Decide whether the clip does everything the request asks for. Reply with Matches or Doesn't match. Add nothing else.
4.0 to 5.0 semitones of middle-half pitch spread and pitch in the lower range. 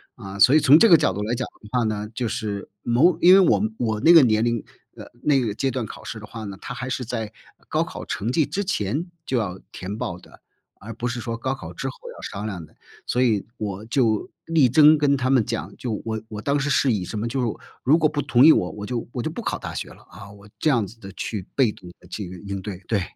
Matches